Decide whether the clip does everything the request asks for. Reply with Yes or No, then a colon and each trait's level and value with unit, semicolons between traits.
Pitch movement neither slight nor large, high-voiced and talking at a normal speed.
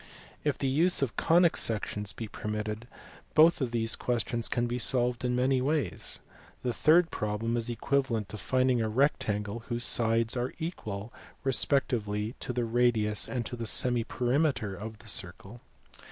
No: average, 3.2 semitones; low, 120 Hz; average, 160 wpm